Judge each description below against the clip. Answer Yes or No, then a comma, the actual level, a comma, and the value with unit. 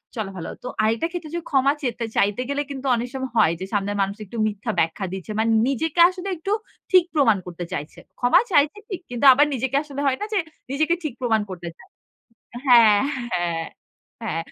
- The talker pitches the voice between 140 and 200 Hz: No, high, 240 Hz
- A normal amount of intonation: No, wide, 6.1 semitones